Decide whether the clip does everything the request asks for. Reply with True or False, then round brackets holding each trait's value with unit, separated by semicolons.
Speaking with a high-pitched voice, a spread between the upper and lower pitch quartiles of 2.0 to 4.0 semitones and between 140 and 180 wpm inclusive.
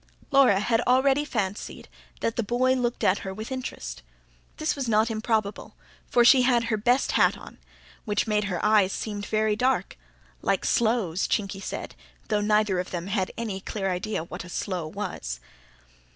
True (215 Hz; 3.7 semitones; 170 wpm)